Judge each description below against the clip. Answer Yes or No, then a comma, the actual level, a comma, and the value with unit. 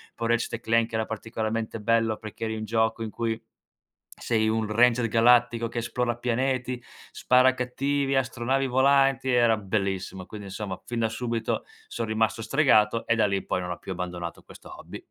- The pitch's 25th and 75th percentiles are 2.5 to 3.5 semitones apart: No, narrow, 2.0 semitones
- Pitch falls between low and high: No, low, 115 Hz